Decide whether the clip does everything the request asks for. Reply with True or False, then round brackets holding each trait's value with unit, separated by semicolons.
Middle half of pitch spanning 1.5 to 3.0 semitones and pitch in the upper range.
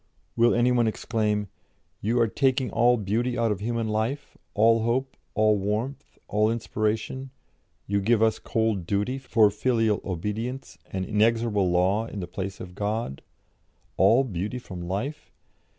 False (2.7 semitones; 110 Hz)